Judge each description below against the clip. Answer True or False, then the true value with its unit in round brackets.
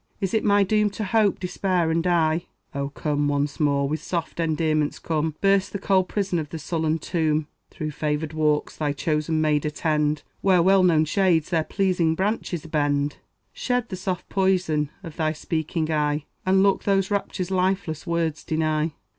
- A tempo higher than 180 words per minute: False (170 wpm)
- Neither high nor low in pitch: True (160 Hz)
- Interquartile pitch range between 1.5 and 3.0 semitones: False (3.7 semitones)